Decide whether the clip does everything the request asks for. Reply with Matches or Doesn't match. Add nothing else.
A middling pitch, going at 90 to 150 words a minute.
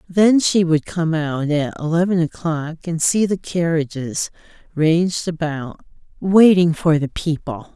Matches